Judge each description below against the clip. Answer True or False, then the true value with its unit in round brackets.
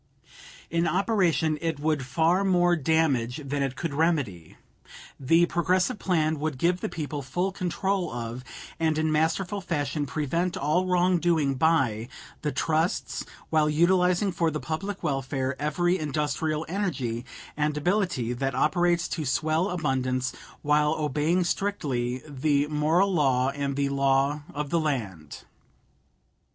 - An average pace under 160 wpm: True (135 wpm)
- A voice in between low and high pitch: True (155 Hz)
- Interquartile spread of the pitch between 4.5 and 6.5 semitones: False (4.0 semitones)